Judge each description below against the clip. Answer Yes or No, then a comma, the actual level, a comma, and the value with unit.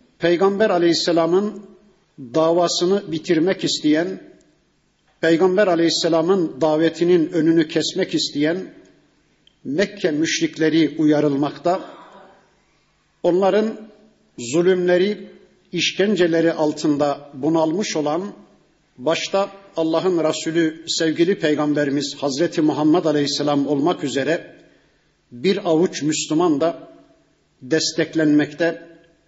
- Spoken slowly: Yes, slow, 70 wpm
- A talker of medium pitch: Yes, medium, 165 Hz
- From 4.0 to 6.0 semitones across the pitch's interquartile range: No, average, 3.3 semitones